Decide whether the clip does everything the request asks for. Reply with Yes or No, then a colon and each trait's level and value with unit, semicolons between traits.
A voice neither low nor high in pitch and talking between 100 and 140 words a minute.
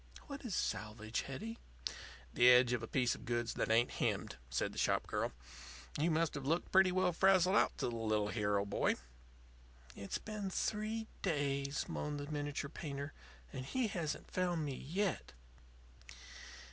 No: medium, 145 Hz; average, 160 wpm